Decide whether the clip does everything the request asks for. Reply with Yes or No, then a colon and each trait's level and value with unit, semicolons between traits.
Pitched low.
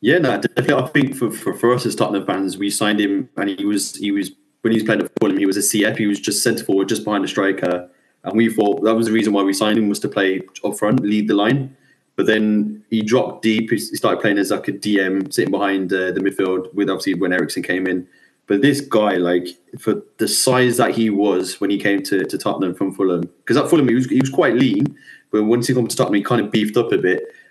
Yes: low, 105 Hz